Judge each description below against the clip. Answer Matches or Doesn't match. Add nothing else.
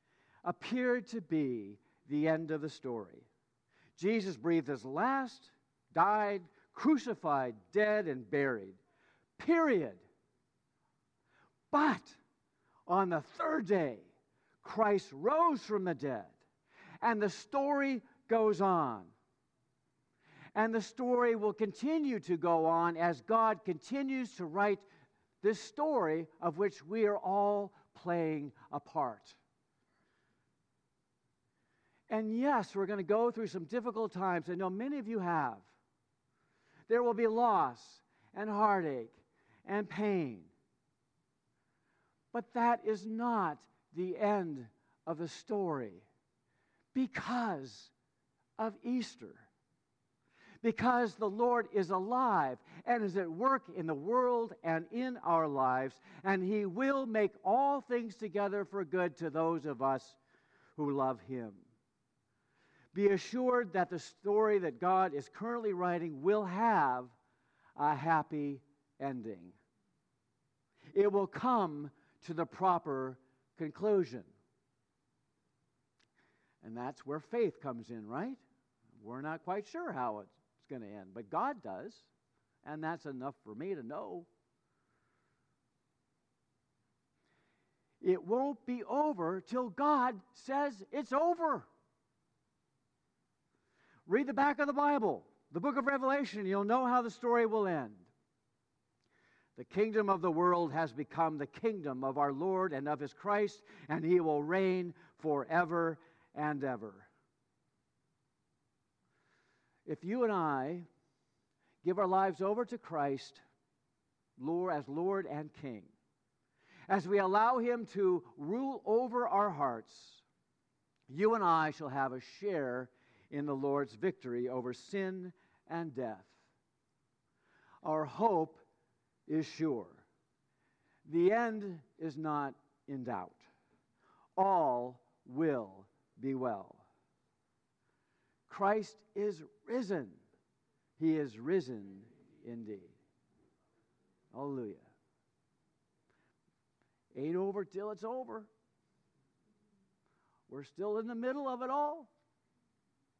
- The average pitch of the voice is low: Doesn't match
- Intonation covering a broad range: Matches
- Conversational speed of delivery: Doesn't match